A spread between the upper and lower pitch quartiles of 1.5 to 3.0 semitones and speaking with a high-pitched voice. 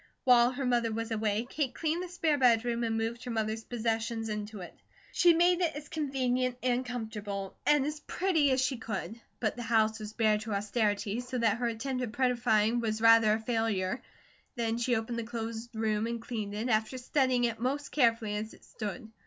Yes: narrow, 2.5 semitones; high, 230 Hz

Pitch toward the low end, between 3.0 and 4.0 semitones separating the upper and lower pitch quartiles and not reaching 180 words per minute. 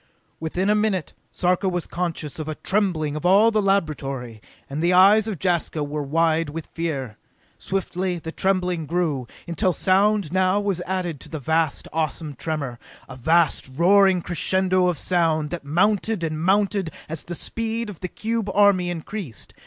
No: medium, 175 Hz; average, 3.6 semitones; average, 165 wpm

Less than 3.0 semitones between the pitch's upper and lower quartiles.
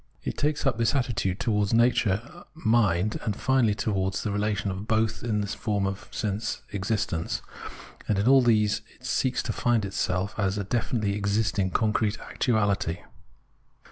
Yes: narrow, 2.6 semitones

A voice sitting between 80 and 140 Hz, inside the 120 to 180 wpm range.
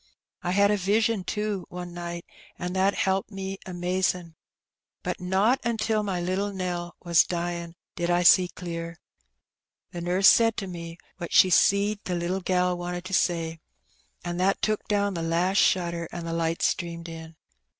No: medium, 180 Hz; average, 170 wpm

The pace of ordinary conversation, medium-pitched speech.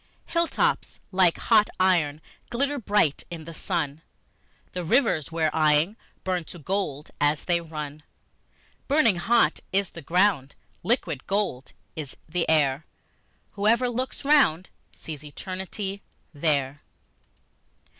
No: slow, 125 wpm; medium, 170 Hz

